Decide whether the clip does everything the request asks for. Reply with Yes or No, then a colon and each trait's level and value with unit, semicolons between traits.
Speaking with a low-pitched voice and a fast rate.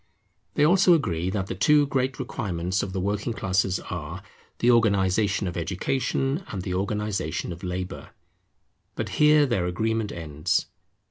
No: low, 100 Hz; average, 145 wpm